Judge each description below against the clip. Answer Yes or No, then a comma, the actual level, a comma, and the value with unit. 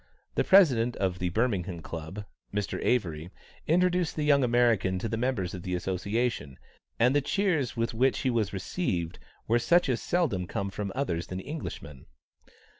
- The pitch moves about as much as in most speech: No, wide, 6.4 semitones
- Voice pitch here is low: Yes, low, 115 Hz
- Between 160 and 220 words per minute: Yes, average, 165 wpm